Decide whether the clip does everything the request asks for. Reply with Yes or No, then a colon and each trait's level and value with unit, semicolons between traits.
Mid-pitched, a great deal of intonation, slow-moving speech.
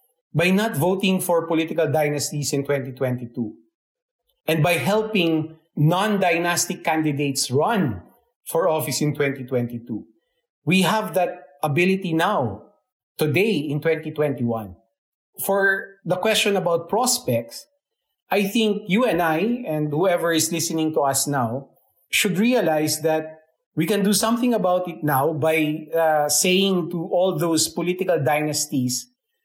No: medium, 170 Hz; average, 4.6 semitones; slow, 125 wpm